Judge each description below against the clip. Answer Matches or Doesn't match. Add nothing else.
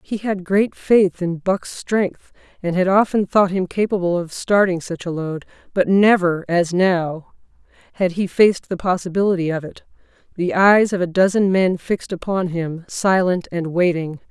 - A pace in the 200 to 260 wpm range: Doesn't match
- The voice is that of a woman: Matches